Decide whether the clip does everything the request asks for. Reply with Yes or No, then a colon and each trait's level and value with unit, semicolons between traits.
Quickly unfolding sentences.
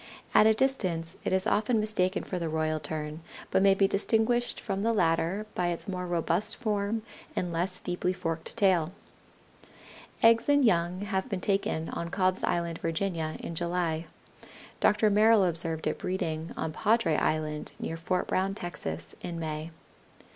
No: average, 160 wpm